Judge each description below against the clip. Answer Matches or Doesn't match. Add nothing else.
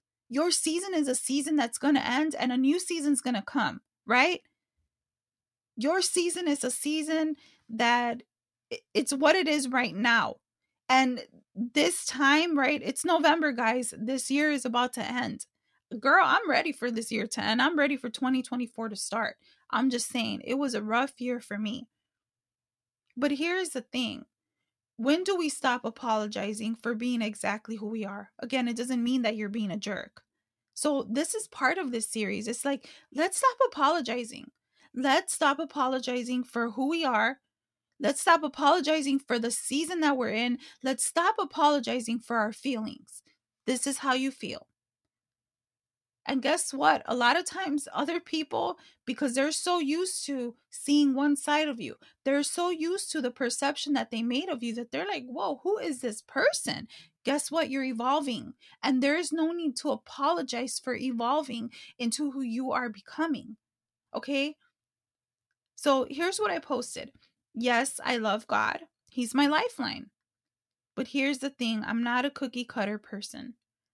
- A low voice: Doesn't match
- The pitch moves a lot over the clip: Doesn't match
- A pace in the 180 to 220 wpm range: Doesn't match